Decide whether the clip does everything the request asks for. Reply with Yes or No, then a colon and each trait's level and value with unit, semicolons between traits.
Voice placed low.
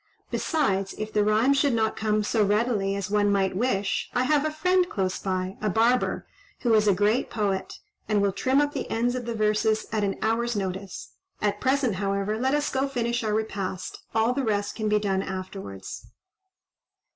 No: high, 215 Hz